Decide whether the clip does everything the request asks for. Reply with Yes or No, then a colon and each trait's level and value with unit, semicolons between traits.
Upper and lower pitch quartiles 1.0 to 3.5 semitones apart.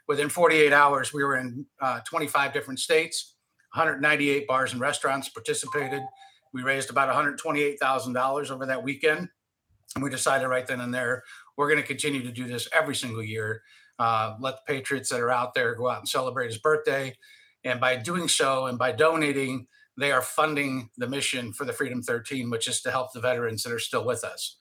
Yes: average, 2.7 semitones